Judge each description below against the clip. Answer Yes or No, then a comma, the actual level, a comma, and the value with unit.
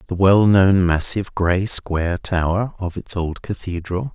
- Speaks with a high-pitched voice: No, very low, 95 Hz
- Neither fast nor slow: Yes, average, 145 wpm